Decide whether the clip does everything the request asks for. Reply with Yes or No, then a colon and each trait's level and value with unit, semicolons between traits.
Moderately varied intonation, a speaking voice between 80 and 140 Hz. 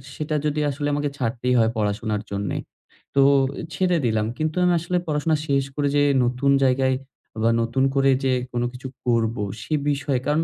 Yes: average, 3.9 semitones; low, 135 Hz